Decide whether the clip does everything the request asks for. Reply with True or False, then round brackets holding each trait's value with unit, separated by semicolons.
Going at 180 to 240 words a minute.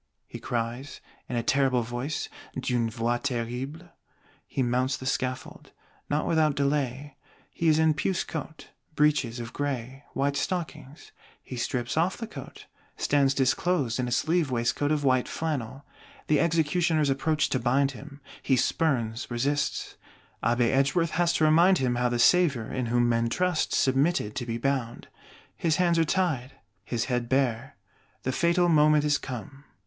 False (155 wpm)